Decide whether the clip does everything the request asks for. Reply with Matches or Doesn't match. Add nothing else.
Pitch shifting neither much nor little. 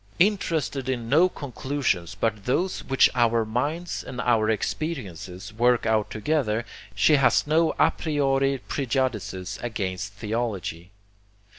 Matches